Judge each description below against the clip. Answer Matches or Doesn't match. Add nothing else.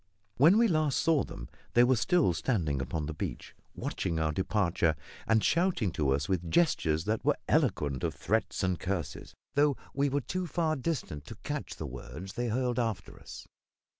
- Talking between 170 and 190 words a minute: Matches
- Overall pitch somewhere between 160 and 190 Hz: Doesn't match